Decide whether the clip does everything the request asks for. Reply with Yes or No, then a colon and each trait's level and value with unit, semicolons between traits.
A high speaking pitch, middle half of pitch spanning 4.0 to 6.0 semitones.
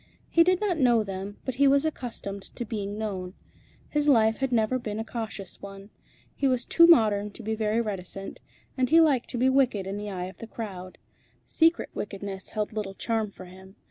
Yes: high, 220 Hz; average, 4.5 semitones